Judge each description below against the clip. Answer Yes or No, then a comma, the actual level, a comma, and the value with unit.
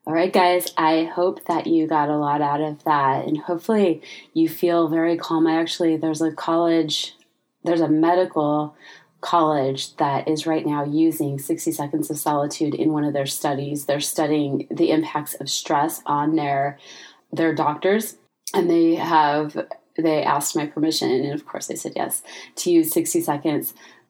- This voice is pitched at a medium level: Yes, medium, 160 Hz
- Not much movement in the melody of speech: Yes, narrow, 2.3 semitones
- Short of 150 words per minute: No, average, 170 wpm